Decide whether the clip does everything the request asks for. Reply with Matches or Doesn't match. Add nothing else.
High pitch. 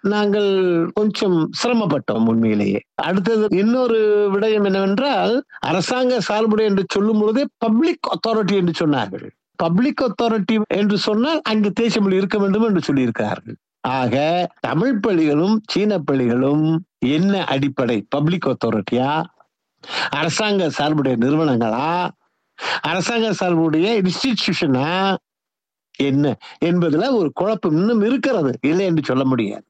Matches